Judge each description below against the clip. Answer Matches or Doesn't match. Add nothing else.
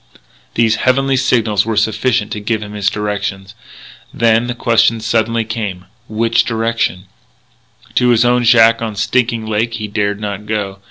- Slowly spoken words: Doesn't match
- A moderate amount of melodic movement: Doesn't match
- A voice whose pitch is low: Matches